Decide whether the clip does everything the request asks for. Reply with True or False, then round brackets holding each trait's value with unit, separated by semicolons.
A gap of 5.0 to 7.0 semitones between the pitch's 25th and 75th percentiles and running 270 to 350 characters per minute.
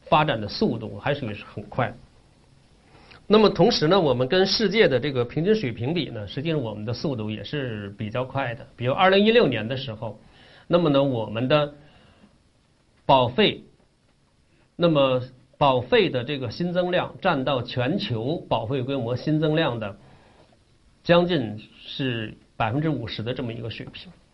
False (5.3 semitones; 245 characters per minute)